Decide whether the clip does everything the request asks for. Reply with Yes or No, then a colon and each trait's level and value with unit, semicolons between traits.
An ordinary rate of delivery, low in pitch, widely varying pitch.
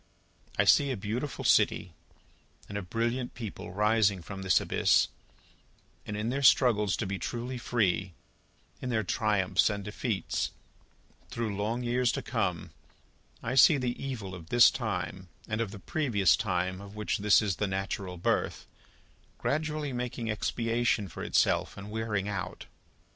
No: average, 150 wpm; low, 105 Hz; average, 3.7 semitones